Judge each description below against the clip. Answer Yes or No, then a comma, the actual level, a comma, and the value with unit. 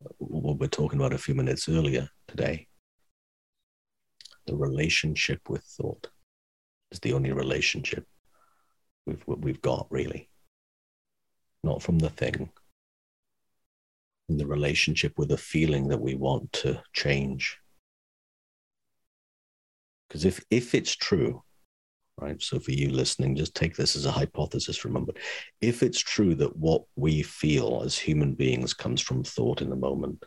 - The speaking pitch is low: Yes, very low, 70 Hz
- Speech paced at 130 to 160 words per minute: Yes, slow, 135 wpm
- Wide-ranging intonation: No, narrow, 2.5 semitones